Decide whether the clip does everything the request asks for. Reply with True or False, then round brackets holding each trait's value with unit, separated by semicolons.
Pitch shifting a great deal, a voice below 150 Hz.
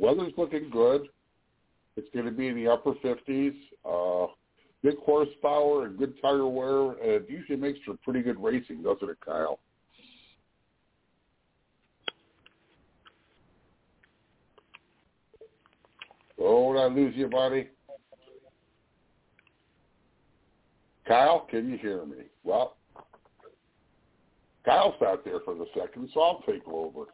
True (5.9 semitones; 140 Hz)